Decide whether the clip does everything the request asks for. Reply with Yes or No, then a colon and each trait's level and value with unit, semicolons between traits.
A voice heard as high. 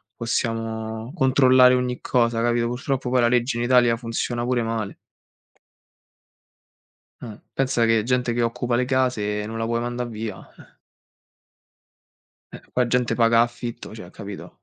No: low, 120 Hz